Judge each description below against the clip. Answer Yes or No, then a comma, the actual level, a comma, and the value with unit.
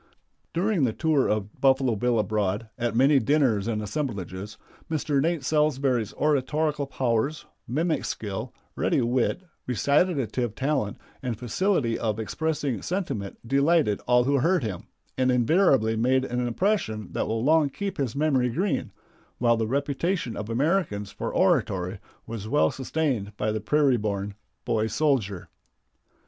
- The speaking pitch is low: Yes, low, 125 Hz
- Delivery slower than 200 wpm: Yes, average, 140 wpm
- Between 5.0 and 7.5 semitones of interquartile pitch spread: Yes, wide, 5.4 semitones